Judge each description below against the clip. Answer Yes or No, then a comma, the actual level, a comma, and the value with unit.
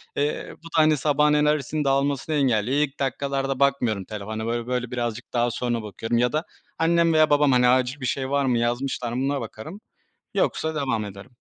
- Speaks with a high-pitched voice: No, low, 130 Hz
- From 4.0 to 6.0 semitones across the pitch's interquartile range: No, average, 3.5 semitones